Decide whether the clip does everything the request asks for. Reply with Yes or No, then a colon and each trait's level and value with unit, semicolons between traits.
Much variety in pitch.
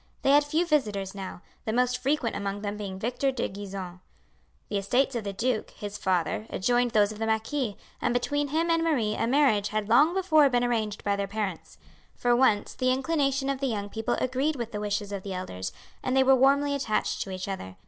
No: average, 5.0 semitones